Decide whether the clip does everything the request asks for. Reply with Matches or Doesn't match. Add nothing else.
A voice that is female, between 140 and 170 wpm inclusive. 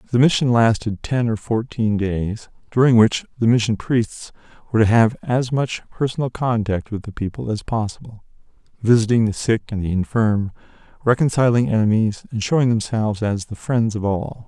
Doesn't match